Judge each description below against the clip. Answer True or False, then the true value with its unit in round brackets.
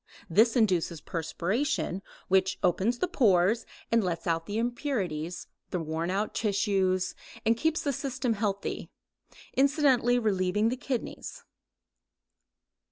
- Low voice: False (210 Hz)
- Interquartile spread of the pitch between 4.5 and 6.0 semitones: True (5.0 semitones)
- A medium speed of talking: False (115 wpm)